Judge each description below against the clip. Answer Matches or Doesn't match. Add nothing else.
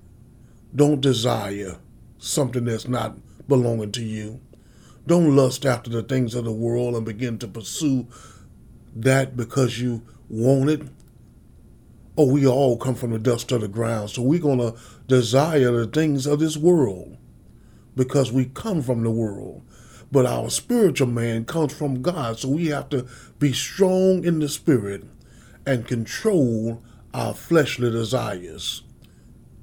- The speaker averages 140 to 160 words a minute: Matches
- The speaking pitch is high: Doesn't match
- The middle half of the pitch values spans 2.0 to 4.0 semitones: Matches